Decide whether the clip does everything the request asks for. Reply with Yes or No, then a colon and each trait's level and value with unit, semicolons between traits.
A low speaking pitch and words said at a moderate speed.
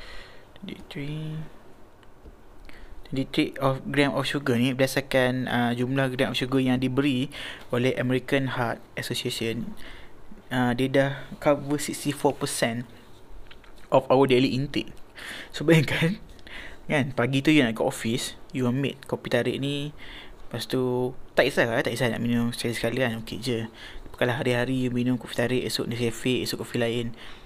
Yes: low, 130 Hz; average, 145 wpm